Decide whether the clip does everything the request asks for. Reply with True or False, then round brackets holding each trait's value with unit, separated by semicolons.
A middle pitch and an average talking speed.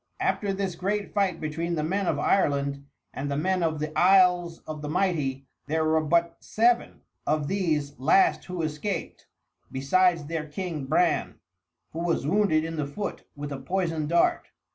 True (165 Hz; 165 wpm)